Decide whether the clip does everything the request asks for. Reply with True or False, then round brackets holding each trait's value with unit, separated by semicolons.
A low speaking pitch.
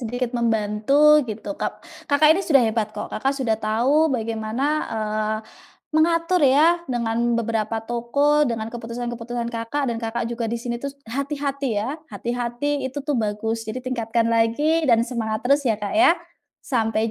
False (235 Hz)